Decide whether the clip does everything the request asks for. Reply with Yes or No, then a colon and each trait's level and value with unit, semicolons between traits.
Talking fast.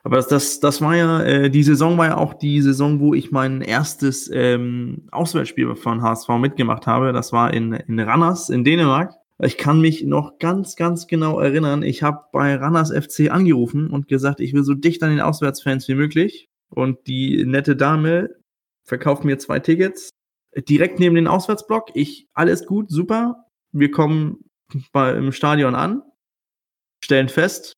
No: average, 175 wpm